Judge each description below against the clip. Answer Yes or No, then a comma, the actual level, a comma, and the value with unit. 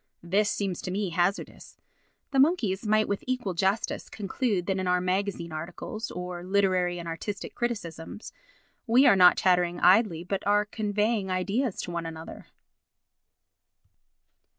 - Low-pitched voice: No, high, 190 Hz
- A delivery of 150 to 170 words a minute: No, average, 140 wpm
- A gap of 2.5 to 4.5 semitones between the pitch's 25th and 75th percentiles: Yes, average, 2.9 semitones